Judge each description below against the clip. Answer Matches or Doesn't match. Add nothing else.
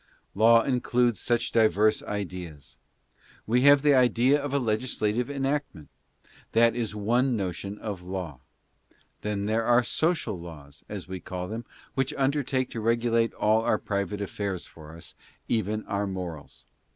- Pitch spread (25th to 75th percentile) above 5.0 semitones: Doesn't match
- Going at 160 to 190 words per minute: Doesn't match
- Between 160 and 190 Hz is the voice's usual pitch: Doesn't match